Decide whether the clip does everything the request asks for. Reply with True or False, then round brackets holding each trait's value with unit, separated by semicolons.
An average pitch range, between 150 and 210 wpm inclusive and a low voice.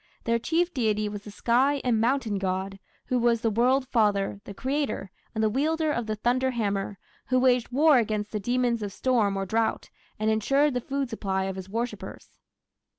False (3.8 semitones; 190 wpm; 230 Hz)